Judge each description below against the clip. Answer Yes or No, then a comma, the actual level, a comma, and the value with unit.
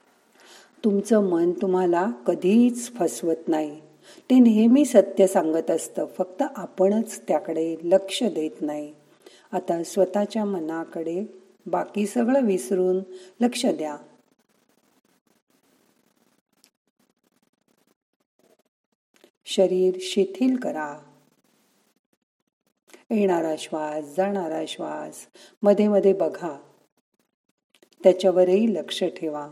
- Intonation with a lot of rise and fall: No, average, 4.2 semitones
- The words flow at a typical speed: No, slow, 75 wpm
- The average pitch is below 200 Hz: Yes, high, 190 Hz